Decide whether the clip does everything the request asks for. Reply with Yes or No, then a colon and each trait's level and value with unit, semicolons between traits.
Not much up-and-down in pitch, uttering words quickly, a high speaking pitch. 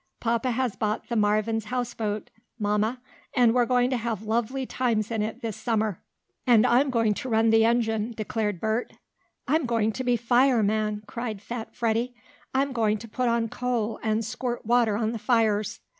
No: narrow, 2.2 semitones; average, 175 wpm; high, 230 Hz